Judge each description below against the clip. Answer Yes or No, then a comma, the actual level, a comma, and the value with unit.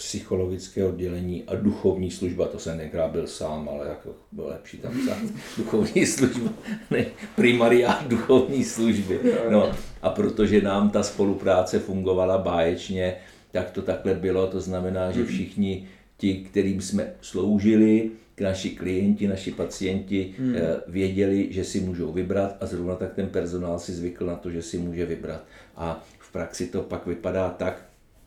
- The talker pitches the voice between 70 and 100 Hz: Yes, very low, 95 Hz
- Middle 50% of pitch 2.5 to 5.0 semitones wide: No, narrow, 2.1 semitones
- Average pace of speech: Yes, average, 150 wpm